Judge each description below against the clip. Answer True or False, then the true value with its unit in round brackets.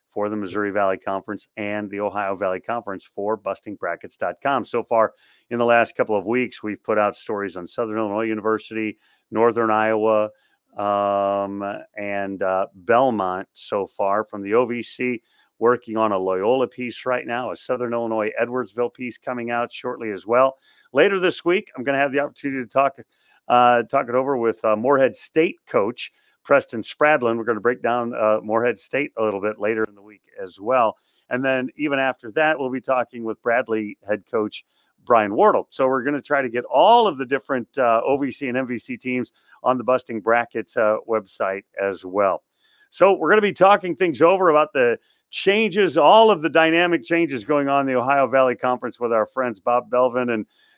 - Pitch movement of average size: True (3.8 semitones)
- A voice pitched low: True (120 Hz)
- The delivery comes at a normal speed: True (190 wpm)